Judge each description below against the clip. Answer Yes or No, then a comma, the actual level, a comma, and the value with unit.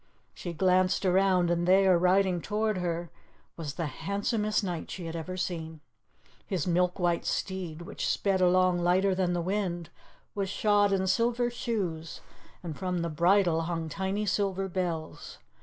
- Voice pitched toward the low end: No, medium, 185 Hz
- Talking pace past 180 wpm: No, average, 155 wpm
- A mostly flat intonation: Yes, narrow, 2.3 semitones